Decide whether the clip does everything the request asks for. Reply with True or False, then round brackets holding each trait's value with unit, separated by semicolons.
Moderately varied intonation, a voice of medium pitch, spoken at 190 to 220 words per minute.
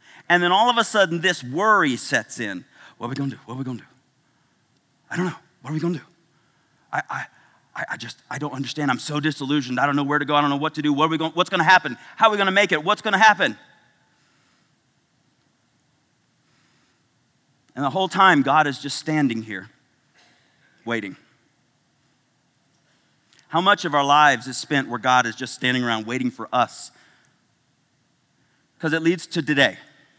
True (3.7 semitones; 145 Hz; 205 wpm)